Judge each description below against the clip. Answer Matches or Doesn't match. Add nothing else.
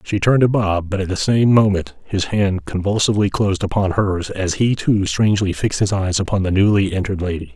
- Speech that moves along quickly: Matches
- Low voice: Matches